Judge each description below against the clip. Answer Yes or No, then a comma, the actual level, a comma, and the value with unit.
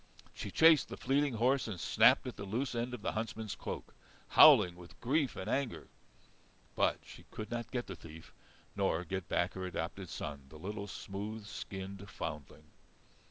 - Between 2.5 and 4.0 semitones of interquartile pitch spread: No, average, 4.9 semitones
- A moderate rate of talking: Yes, average, 170 wpm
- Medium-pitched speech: No, low, 100 Hz